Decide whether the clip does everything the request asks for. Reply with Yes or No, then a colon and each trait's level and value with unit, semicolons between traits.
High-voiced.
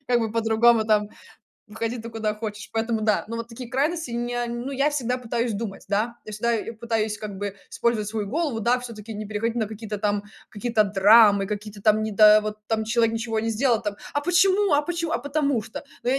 Yes: high, 225 Hz